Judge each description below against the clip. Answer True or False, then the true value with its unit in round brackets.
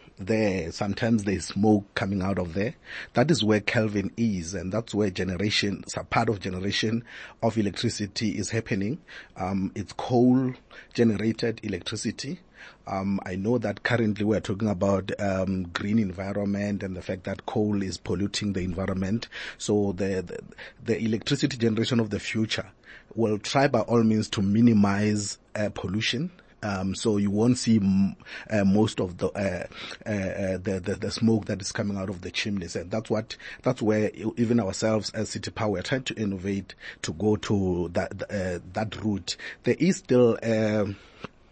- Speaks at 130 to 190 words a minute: True (175 wpm)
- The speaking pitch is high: False (105 Hz)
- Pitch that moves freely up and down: False (2.4 semitones)